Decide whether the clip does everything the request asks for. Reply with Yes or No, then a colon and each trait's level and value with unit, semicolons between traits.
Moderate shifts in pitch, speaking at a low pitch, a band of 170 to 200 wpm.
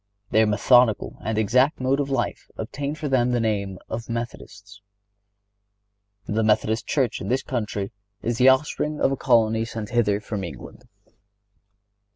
No: average, 3.5 semitones; low, 115 Hz; average, 150 wpm